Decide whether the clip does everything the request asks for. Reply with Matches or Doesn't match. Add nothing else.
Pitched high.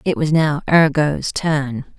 Doesn't match